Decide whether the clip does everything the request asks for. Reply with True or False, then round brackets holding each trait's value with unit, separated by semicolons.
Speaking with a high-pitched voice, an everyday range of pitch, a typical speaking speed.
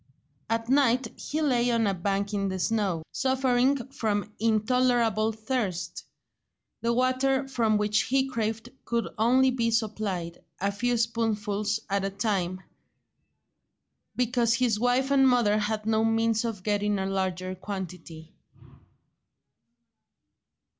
False (225 Hz; 3.4 semitones; 125 wpm)